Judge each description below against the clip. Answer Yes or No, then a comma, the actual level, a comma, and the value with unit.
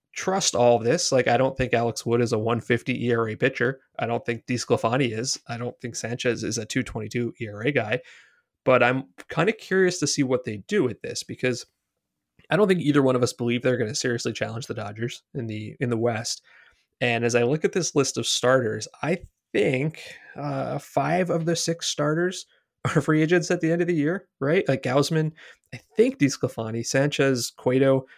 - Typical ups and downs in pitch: Yes, average, 4.6 semitones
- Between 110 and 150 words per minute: No, fast, 205 wpm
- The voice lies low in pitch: Yes, low, 130 Hz